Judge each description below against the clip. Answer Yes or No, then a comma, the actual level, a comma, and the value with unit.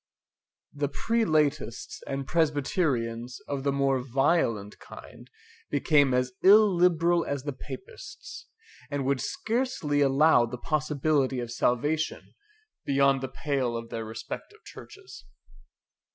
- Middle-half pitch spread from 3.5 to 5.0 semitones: Yes, average, 4.0 semitones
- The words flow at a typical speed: No, slow, 110 wpm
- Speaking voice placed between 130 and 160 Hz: Yes, medium, 140 Hz